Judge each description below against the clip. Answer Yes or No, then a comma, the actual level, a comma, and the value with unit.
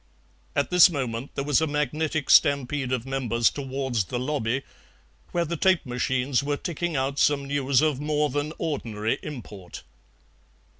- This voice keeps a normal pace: Yes, average, 150 wpm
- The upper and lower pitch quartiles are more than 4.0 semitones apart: No, average, 3.0 semitones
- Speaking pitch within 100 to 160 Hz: Yes, medium, 140 Hz